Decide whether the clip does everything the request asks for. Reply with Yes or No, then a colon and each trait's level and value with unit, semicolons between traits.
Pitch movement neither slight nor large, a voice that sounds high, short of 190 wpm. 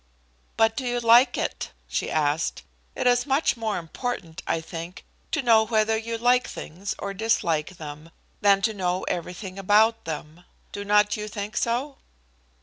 Yes: average, 4.8 semitones; high, 210 Hz; average, 160 wpm